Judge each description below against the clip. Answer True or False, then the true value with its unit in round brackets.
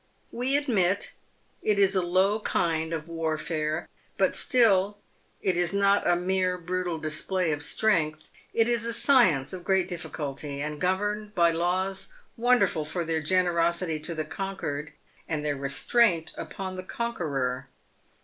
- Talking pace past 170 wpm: False (145 wpm)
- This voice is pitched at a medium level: True (180 Hz)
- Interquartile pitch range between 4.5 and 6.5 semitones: False (4.0 semitones)